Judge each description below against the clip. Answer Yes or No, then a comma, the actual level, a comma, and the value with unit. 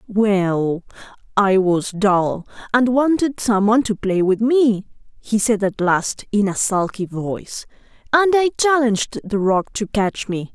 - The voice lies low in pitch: No, high, 215 Hz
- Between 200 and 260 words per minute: No, average, 150 wpm